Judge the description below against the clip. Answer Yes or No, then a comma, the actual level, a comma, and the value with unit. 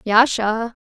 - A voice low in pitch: No, high, 225 Hz